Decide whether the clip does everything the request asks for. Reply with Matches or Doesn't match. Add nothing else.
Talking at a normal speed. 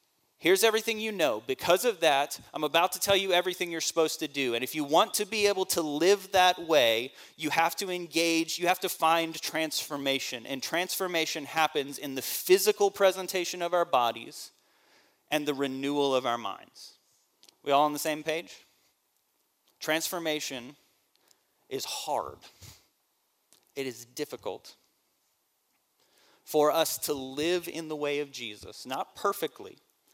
Matches